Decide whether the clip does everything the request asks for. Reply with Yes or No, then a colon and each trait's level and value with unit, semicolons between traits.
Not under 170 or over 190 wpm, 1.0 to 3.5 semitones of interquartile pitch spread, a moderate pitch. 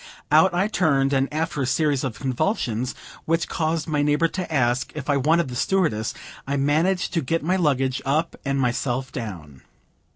No: average, 175 wpm; average, 4.0 semitones; medium, 145 Hz